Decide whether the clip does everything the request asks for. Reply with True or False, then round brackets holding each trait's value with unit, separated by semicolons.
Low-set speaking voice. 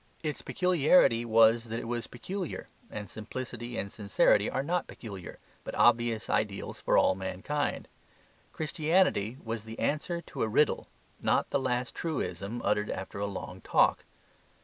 True (115 Hz)